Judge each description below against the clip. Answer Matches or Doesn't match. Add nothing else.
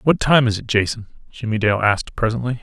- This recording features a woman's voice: Doesn't match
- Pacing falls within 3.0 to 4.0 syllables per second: Doesn't match